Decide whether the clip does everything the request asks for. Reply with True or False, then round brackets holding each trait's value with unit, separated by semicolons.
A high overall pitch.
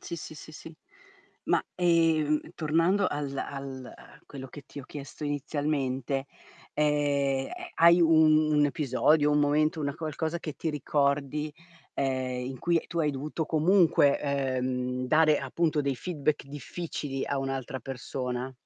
False (145 Hz)